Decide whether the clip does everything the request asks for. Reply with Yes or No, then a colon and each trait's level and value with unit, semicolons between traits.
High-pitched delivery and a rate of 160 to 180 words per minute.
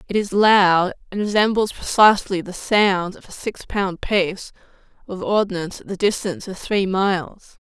Yes: high, 195 Hz; average, 165 wpm